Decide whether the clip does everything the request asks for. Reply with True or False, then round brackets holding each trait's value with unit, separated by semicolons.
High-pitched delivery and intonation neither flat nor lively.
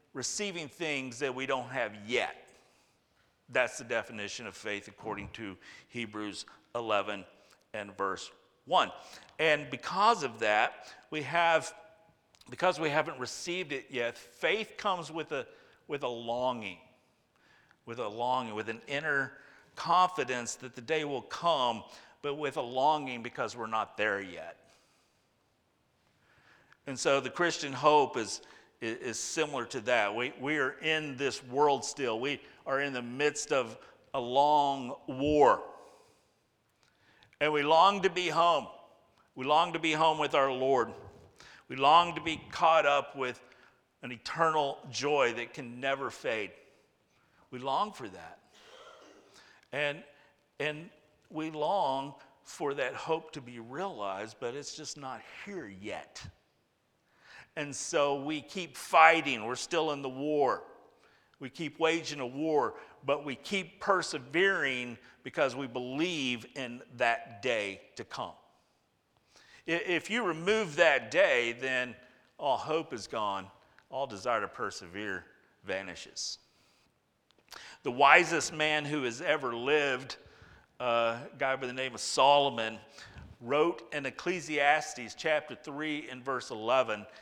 False (140 Hz; 4.1 semitones)